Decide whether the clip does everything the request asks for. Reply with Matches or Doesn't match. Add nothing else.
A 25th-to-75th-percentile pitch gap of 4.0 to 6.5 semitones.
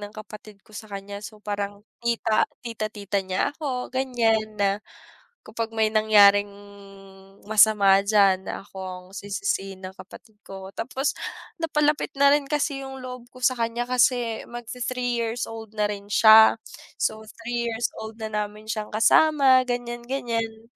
Doesn't match